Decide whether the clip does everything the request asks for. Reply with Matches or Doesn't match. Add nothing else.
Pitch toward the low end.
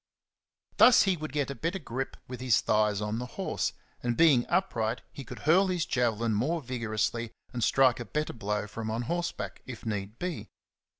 Matches